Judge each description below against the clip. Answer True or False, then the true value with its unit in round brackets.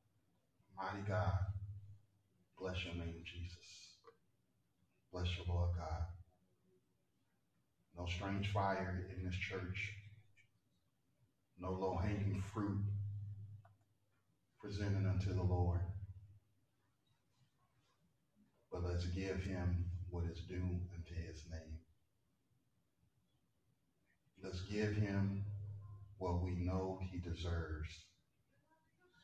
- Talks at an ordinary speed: False (85 wpm)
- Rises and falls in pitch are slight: True (2.3 semitones)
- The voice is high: False (95 Hz)